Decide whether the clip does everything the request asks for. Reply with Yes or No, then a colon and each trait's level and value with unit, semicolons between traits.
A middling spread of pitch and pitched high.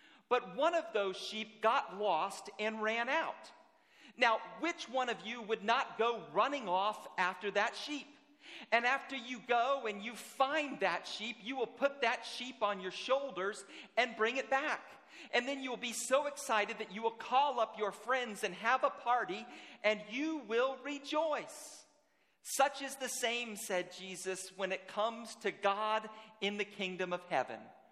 Yes: average, 4.4 semitones; high, 230 Hz